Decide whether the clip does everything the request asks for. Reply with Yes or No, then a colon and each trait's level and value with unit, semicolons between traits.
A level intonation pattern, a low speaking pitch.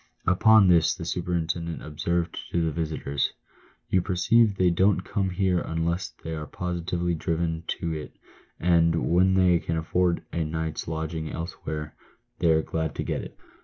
Yes: narrow, 2.0 semitones; very low, 85 Hz